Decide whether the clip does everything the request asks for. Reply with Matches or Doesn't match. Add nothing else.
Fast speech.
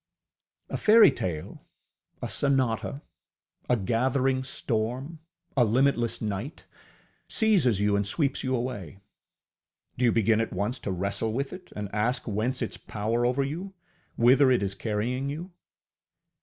Doesn't match